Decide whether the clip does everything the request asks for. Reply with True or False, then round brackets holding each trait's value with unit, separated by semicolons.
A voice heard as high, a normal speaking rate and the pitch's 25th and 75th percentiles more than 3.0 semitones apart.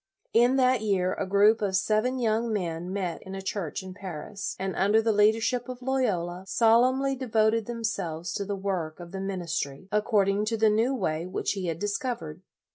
True (205 Hz; 195 wpm; 3.6 semitones)